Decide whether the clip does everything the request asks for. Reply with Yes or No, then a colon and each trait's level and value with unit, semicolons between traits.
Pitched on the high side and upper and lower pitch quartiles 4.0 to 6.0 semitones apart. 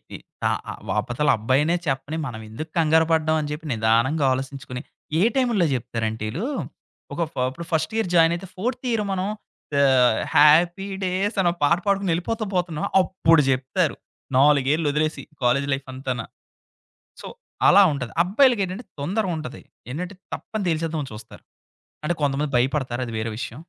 No: medium, 155 Hz; average, 5.3 semitones